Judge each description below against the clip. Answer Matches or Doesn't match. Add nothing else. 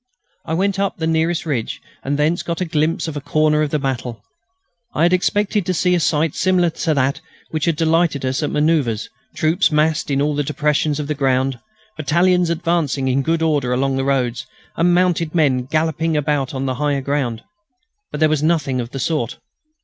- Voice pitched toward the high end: Doesn't match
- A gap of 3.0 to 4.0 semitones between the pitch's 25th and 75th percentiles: Matches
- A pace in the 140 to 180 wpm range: Doesn't match